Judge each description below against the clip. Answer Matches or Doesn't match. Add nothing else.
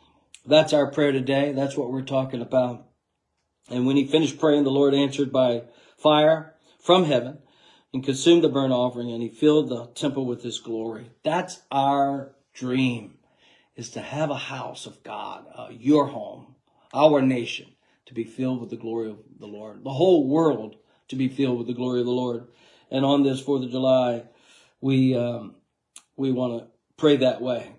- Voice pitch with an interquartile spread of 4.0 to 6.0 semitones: Doesn't match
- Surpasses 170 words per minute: Matches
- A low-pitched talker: Matches